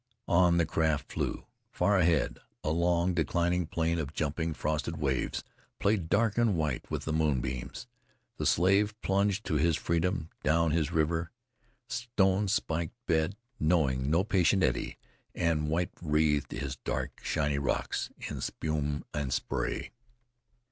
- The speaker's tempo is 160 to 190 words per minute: No, average, 140 wpm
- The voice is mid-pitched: No, very low, 80 Hz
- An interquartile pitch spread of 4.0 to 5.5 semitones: No, average, 2.9 semitones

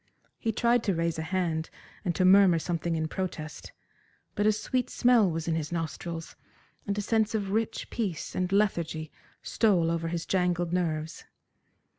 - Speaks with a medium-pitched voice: Yes, medium, 175 Hz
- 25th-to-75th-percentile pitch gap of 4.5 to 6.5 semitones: No, average, 3.8 semitones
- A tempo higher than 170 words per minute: No, average, 165 wpm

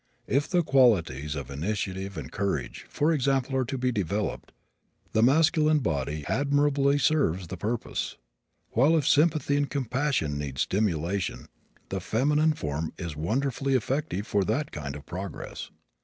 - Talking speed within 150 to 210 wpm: No, average, 140 wpm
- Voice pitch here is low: Yes, low, 110 Hz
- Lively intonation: Yes, wide, 9.0 semitones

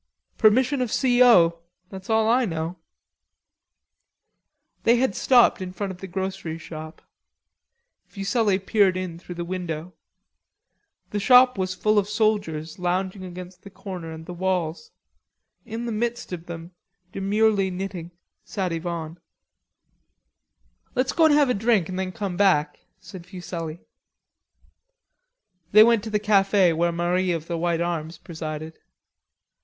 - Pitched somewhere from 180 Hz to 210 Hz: Yes, medium, 185 Hz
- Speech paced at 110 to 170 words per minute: Yes, average, 140 wpm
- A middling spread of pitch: Yes, average, 3.8 semitones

